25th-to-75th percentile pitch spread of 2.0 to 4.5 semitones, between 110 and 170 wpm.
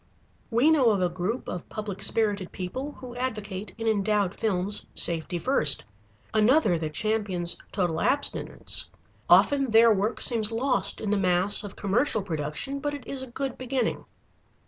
No: average, 5.1 semitones; average, 155 wpm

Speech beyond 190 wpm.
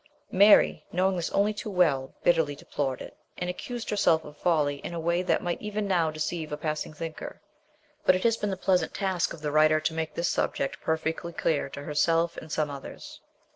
Yes: fast, 205 wpm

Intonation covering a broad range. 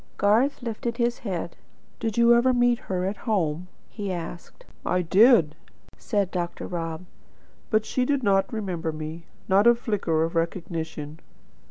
Yes: wide, 5.9 semitones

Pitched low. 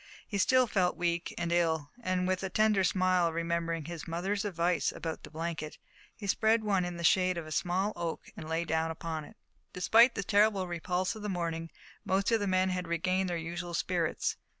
No: medium, 175 Hz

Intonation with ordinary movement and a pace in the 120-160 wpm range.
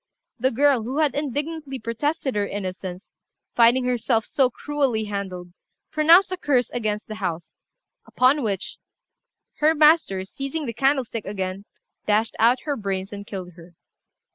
No: wide, 6.1 semitones; average, 140 wpm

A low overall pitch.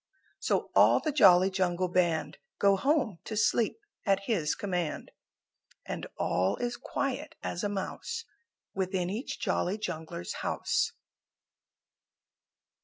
No: high, 195 Hz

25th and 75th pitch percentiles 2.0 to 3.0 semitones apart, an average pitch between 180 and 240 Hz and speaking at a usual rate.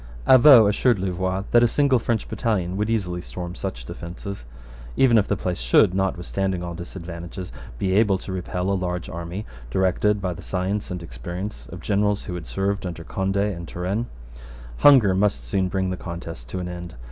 No: narrow, 2.6 semitones; very low, 95 Hz; average, 180 wpm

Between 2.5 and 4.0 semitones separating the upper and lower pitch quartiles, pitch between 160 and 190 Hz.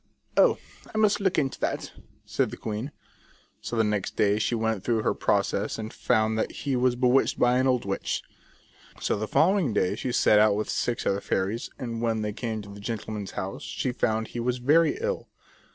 No: average, 3.1 semitones; low, 115 Hz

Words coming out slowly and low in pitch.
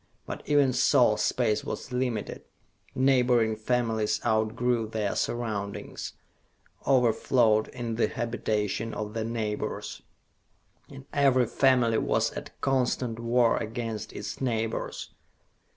Yes: slow, 105 wpm; low, 115 Hz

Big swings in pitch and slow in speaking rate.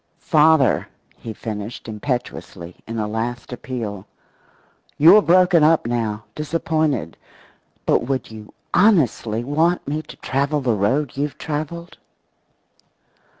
Yes: wide, 5.8 semitones; slow, 110 wpm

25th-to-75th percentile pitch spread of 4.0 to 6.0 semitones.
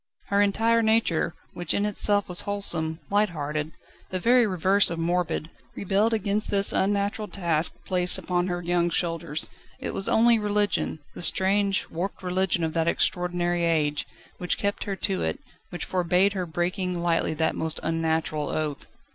No: average, 3.4 semitones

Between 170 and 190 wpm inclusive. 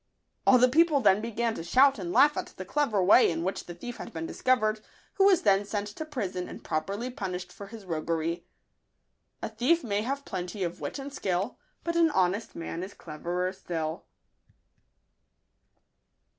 Yes: average, 175 wpm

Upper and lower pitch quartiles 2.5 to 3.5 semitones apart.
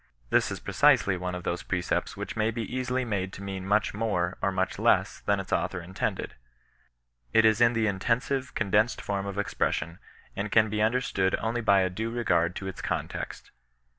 Yes: average, 3.2 semitones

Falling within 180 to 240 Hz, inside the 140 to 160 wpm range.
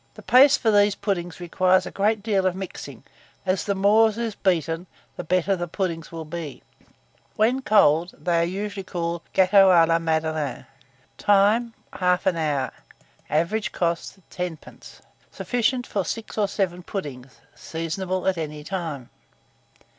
Yes: medium, 185 Hz; average, 150 wpm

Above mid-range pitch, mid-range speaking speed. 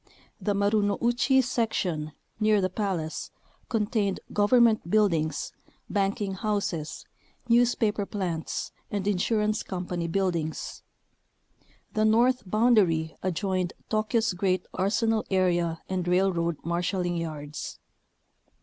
No: high, 195 Hz; slow, 95 wpm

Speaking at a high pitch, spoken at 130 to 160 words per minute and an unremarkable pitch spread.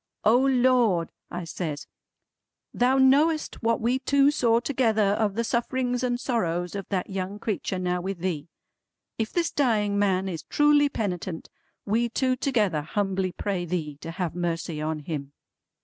No: high, 205 Hz; average, 155 wpm; wide, 5.9 semitones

